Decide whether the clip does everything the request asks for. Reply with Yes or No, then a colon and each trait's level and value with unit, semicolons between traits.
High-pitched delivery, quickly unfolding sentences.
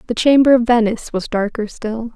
No: high, 230 Hz; average, 195 wpm